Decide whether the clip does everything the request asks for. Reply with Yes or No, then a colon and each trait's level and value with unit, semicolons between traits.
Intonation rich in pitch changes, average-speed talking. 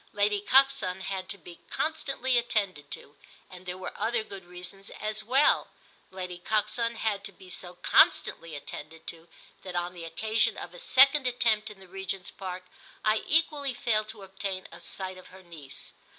No: average, 3.8 semitones; average, 175 wpm